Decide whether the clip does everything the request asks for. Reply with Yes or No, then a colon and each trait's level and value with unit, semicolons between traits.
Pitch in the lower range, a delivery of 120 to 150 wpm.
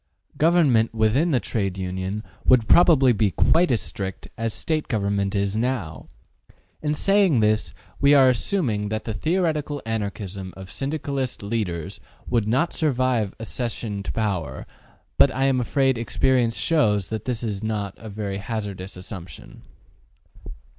Yes: low, 110 Hz; average, 140 wpm